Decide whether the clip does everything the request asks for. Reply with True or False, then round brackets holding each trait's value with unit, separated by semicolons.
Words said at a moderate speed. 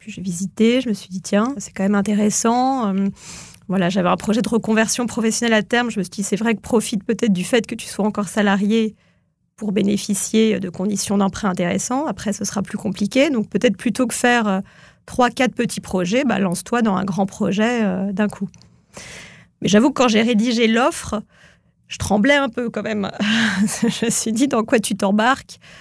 True (205 wpm)